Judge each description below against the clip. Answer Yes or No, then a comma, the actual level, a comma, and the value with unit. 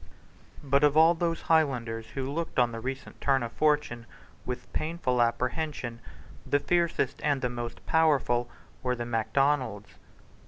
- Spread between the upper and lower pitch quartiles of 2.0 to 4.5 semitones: Yes, average, 4.0 semitones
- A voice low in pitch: Yes, low, 130 Hz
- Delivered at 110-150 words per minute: Yes, average, 145 wpm